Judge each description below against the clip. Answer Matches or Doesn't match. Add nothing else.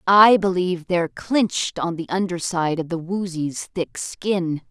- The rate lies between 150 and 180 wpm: Matches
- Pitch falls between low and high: Matches